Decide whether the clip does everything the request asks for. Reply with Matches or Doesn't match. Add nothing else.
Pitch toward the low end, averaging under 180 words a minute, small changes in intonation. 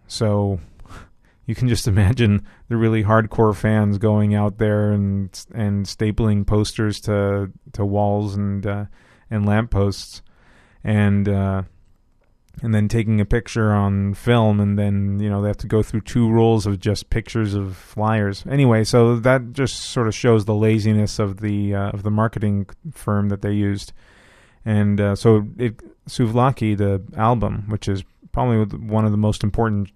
Matches